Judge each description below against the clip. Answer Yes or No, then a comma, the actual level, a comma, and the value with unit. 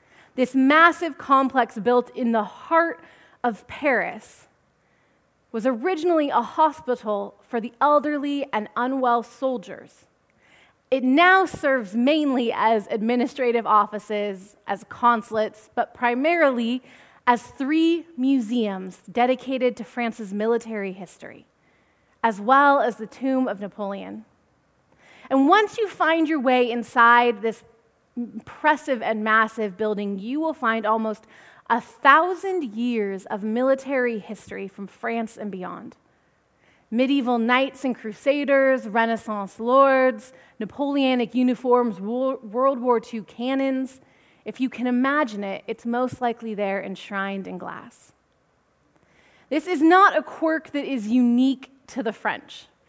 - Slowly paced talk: Yes, slow, 120 wpm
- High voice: Yes, high, 245 Hz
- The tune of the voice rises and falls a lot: No, average, 3.5 semitones